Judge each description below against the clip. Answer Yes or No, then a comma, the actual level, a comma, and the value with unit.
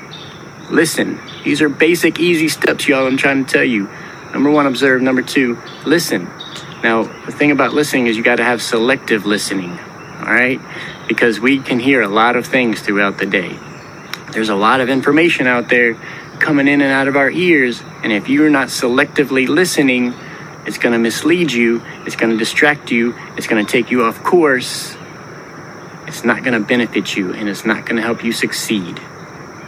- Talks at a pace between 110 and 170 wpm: No, average, 190 wpm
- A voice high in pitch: No, low, 130 Hz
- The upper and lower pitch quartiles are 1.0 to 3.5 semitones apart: No, average, 4.3 semitones